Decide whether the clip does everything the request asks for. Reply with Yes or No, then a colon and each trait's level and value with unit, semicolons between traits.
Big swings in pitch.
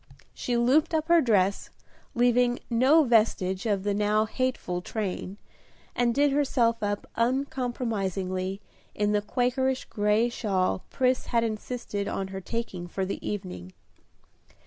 No: average, 4.1 semitones